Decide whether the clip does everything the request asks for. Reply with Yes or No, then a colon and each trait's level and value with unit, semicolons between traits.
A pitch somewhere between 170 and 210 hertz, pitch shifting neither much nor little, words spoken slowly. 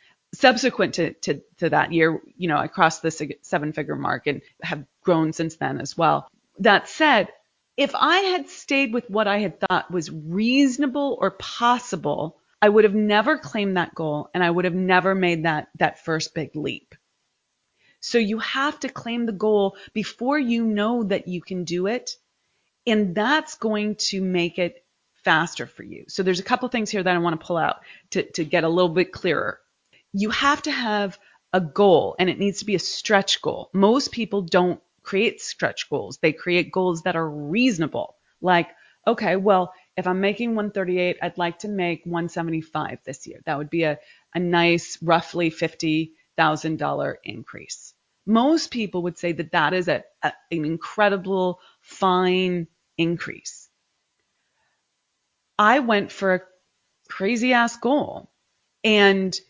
No: medium, 185 Hz; average, 4.5 semitones; average, 170 wpm